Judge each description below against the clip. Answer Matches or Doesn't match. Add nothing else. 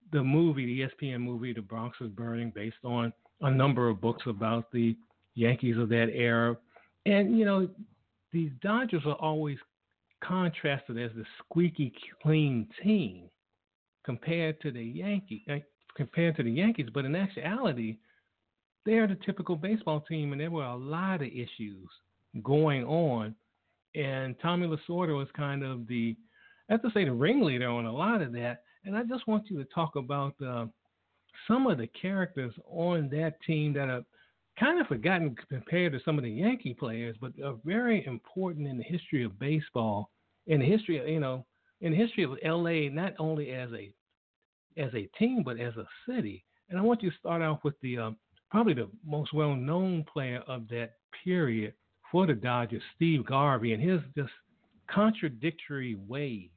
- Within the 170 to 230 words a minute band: Matches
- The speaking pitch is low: Doesn't match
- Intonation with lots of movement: Matches